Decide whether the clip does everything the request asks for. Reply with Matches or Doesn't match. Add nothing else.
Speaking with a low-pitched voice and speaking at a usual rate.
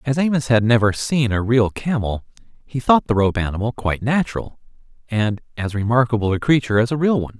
Matches